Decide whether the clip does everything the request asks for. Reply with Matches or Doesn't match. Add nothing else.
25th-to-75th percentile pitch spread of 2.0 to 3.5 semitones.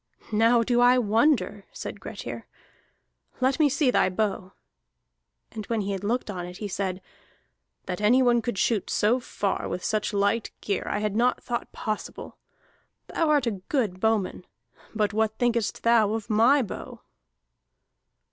Matches